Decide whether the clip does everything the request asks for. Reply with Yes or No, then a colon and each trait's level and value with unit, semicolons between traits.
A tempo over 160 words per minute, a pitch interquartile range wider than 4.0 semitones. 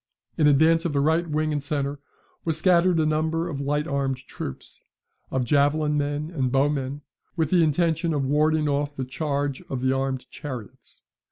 No: average, 175 wpm; narrow, 2.4 semitones